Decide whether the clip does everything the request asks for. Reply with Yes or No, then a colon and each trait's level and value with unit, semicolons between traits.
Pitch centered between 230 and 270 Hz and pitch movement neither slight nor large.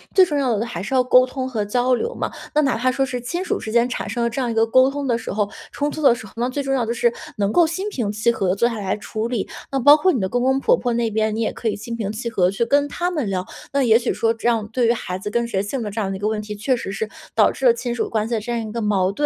Yes: high, 235 Hz; average, 3.2 semitones